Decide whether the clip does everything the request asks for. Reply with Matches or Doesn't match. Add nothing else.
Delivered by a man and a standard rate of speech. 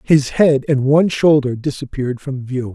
Matches